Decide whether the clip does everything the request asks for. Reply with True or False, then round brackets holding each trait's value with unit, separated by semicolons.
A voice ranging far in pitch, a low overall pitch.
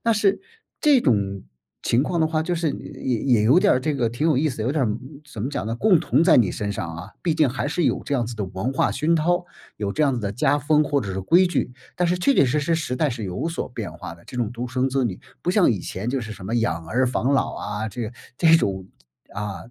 True (6.6 semitones; 130 Hz)